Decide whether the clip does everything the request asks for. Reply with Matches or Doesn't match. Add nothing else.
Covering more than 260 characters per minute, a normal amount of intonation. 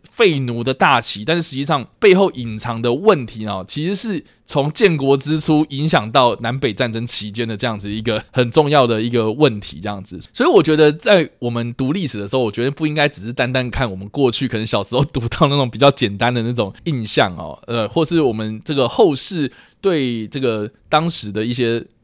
Matches